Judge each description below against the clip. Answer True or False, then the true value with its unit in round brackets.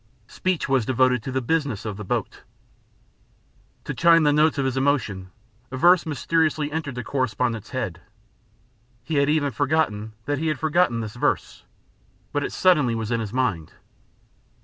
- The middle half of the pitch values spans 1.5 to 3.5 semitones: False (5.2 semitones)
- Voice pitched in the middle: False (130 Hz)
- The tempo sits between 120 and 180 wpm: True (165 wpm)